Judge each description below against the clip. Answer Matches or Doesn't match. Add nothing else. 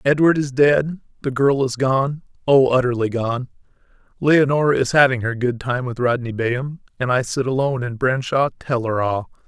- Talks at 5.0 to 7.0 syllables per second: Matches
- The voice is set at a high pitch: Doesn't match